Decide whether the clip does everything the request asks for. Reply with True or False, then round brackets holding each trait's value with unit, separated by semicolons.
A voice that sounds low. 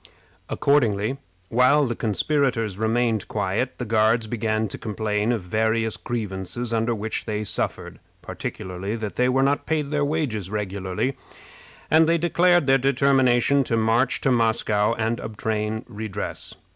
True (115 Hz)